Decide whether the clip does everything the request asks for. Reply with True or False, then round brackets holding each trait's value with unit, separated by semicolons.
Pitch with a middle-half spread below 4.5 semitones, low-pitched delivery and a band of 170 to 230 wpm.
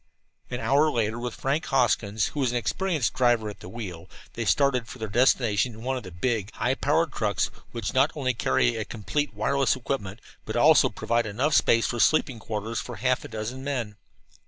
True (3.7 semitones; 120 Hz; 200 wpm)